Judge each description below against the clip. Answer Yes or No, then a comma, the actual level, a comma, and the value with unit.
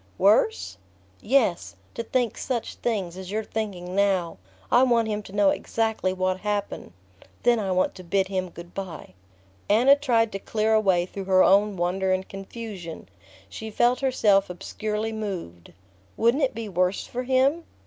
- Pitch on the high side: Yes, high, 205 Hz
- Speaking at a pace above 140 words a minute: Yes, average, 160 wpm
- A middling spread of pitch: Yes, average, 3.5 semitones